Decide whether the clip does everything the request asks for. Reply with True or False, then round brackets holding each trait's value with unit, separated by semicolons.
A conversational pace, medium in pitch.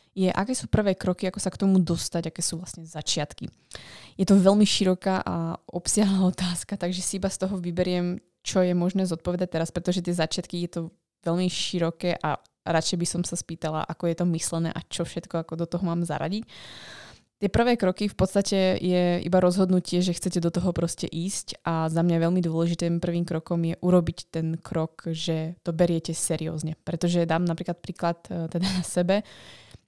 False (185 wpm; 175 Hz)